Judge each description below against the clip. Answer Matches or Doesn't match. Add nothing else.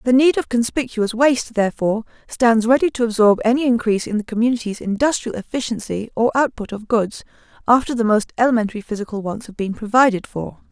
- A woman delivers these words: Matches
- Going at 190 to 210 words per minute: Doesn't match